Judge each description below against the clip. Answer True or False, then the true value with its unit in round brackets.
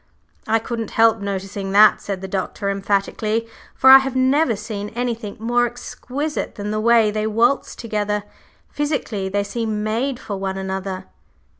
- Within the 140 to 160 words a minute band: True (155 wpm)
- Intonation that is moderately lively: True (3.0 semitones)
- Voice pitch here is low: False (215 Hz)